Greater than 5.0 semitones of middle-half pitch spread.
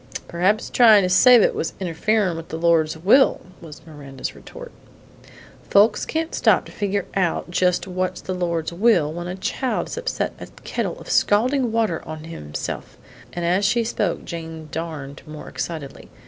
No: average, 4.5 semitones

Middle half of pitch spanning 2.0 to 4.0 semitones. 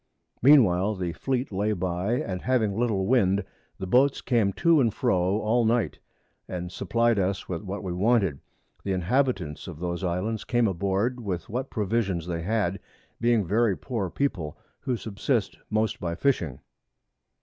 No: average, 4.6 semitones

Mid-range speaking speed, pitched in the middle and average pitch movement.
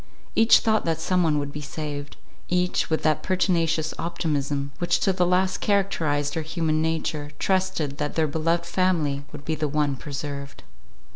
Yes: average, 160 wpm; medium, 160 Hz; average, 3.5 semitones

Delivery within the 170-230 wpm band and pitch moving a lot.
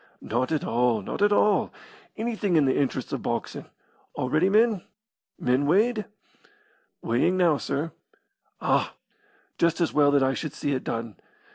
No: average, 150 wpm; wide, 7.4 semitones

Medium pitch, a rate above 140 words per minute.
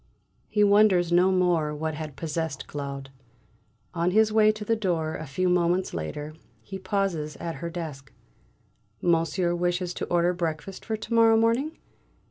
Yes: medium, 175 Hz; average, 155 wpm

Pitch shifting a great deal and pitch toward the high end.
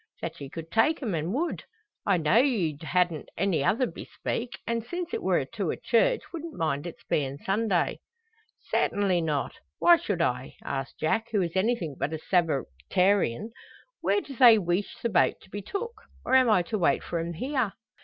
Yes: wide, 6.4 semitones; high, 195 Hz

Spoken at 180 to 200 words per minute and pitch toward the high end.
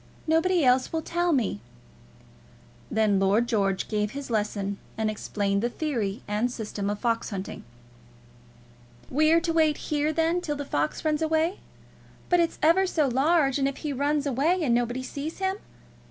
No: average, 165 wpm; very high, 275 Hz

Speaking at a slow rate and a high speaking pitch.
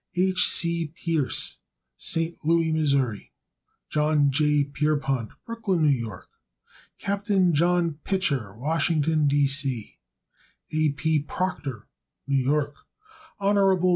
No: slow, 105 wpm; medium, 150 Hz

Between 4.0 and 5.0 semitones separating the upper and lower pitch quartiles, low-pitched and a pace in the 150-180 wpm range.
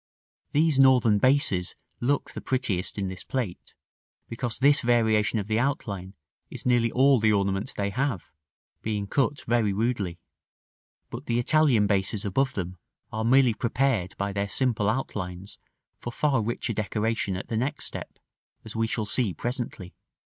Yes: average, 4.4 semitones; low, 110 Hz; average, 155 wpm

